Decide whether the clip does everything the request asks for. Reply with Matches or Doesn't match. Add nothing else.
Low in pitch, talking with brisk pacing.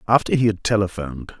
Doesn't match